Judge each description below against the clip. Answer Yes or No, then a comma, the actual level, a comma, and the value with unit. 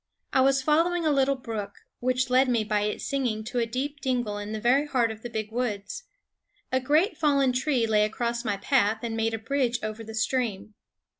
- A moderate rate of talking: No, fast, 210 wpm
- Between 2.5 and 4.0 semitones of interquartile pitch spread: Yes, average, 3.5 semitones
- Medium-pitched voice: No, high, 240 Hz